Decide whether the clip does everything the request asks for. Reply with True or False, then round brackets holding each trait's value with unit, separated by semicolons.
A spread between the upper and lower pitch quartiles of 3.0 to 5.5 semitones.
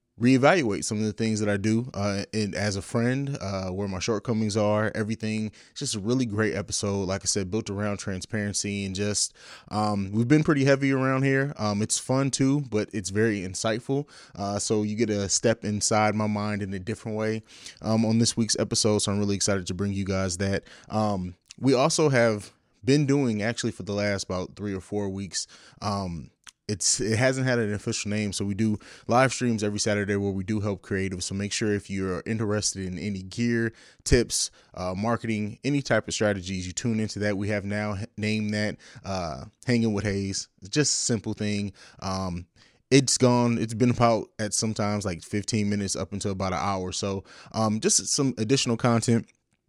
False (2.5 semitones)